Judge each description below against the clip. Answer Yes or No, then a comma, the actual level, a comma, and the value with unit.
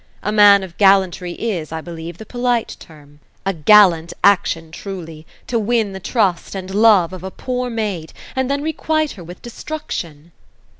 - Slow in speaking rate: No, average, 165 wpm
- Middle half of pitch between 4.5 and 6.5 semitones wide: Yes, average, 5.0 semitones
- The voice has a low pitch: No, high, 195 Hz